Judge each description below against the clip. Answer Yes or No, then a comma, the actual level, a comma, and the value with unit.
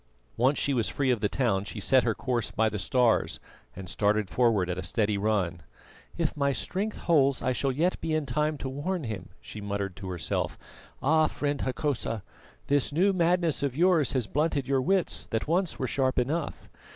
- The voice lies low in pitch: Yes, low, 130 Hz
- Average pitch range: No, wide, 5.9 semitones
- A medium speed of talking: Yes, average, 195 wpm